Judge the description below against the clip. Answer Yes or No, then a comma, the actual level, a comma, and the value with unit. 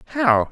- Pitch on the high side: No, medium, 175 Hz